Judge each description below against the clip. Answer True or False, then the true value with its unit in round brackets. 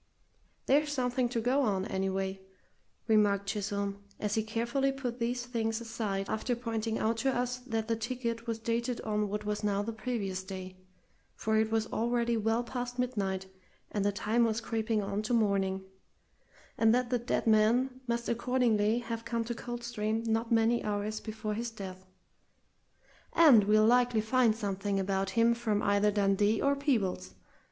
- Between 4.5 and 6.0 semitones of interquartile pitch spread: False (2.5 semitones)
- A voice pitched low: False (225 Hz)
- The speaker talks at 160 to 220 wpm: True (165 wpm)